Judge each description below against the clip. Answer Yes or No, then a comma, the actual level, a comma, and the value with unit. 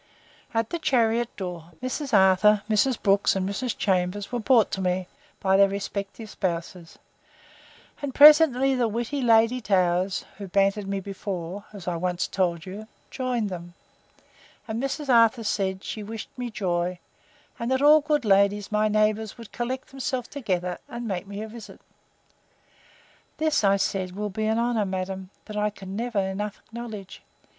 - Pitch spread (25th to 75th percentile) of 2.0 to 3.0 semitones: No, average, 3.8 semitones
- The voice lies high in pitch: Yes, high, 210 Hz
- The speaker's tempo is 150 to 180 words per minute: Yes, average, 165 wpm